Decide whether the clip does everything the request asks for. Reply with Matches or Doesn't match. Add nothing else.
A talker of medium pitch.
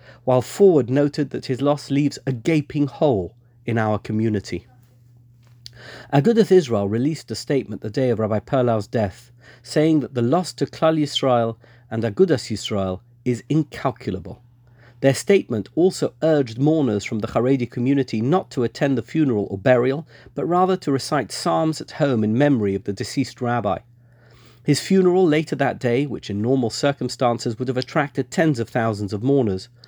Doesn't match